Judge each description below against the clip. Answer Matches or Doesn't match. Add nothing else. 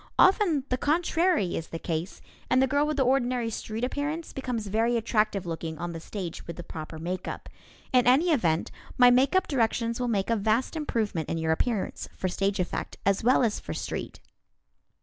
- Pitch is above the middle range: Matches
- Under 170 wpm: Doesn't match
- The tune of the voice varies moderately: Doesn't match